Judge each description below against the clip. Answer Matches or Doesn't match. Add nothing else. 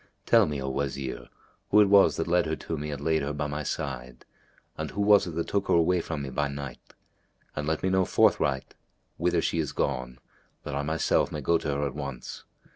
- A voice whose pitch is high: Doesn't match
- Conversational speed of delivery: Doesn't match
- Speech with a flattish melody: Doesn't match